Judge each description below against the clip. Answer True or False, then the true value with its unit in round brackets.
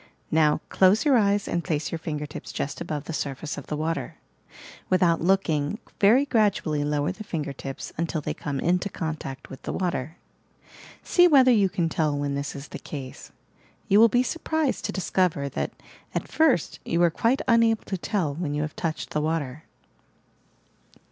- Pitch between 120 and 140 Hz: False (165 Hz)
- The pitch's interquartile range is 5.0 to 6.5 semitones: True (5.3 semitones)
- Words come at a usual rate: True (180 wpm)